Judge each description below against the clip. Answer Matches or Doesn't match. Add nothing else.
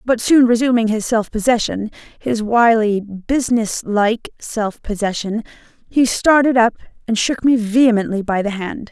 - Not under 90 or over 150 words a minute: Matches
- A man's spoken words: Doesn't match